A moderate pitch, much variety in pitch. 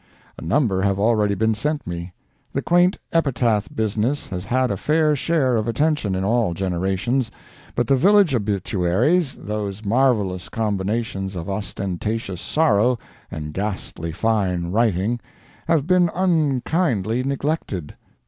No: low, 110 Hz; wide, 6.0 semitones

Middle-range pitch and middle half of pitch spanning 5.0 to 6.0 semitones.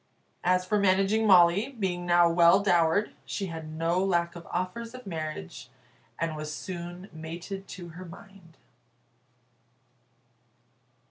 No: medium, 175 Hz; narrow, 2.6 semitones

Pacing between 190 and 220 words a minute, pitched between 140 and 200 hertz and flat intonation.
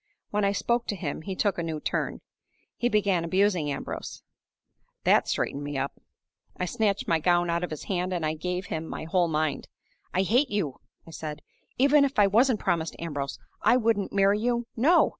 No: average, 195 wpm; medium, 185 Hz; average, 4.7 semitones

